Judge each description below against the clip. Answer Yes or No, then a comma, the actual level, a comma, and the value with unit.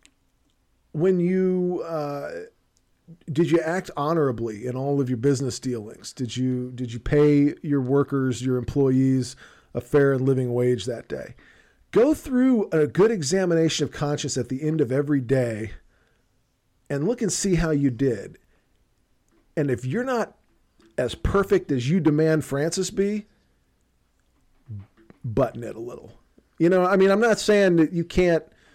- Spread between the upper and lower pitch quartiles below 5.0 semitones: No, wide, 5.6 semitones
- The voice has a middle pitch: Yes, medium, 145 Hz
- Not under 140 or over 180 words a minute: Yes, average, 155 wpm